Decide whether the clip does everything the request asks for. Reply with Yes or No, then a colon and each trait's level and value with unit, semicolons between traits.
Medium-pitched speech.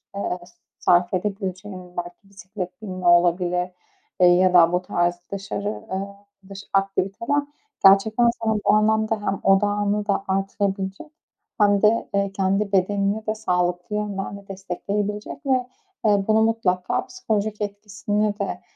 No: high, 200 Hz